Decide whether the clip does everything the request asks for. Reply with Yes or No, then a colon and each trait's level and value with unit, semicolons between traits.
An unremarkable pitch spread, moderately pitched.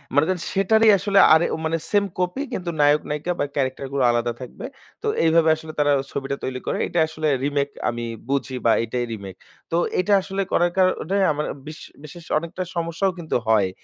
Yes: average, 4.6 semitones; medium, 155 Hz